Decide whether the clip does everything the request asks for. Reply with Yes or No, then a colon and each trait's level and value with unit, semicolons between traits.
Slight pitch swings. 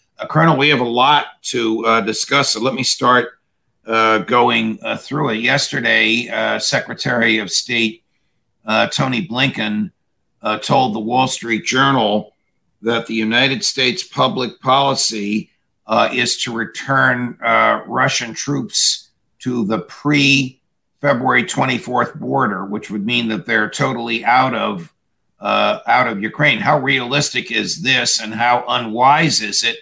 Yes: narrow, 1.8 semitones